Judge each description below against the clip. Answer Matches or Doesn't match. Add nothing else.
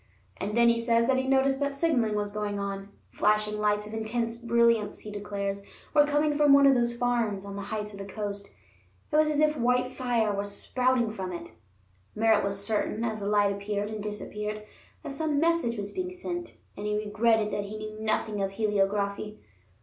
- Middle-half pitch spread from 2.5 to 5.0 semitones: Matches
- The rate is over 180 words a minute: Matches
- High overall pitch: Matches